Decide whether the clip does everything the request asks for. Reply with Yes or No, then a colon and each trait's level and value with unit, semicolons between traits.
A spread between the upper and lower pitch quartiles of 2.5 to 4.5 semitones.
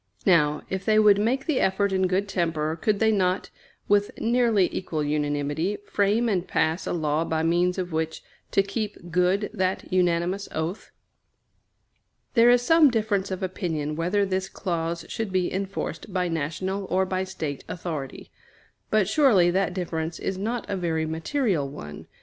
Yes: average, 3.7 semitones